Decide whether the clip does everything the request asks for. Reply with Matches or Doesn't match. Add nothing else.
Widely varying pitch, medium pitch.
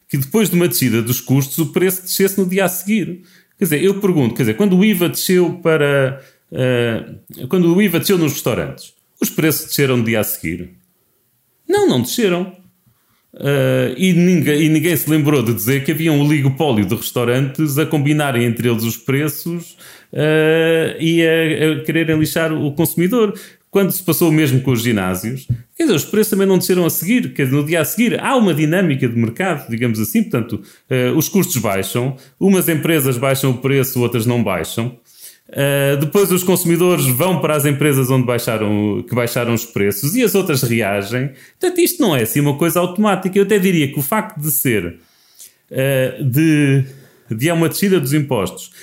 Matches